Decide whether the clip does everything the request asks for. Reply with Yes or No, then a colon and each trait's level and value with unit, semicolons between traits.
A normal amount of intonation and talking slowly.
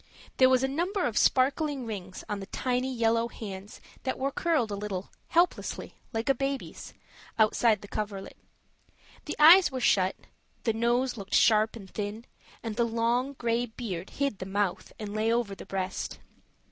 No: average, 4.0 semitones; average, 170 wpm